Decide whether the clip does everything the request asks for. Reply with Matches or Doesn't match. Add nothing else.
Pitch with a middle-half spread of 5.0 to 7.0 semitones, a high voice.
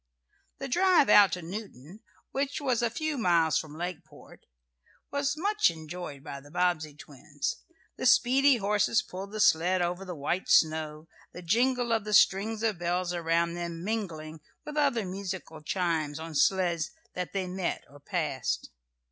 Doesn't match